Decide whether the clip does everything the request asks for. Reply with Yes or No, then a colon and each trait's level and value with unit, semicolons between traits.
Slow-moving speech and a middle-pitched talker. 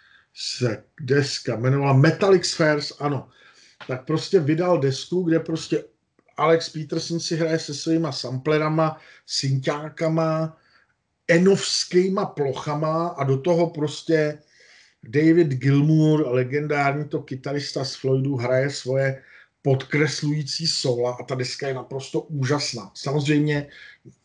Yes: slow, 110 wpm; medium, 150 Hz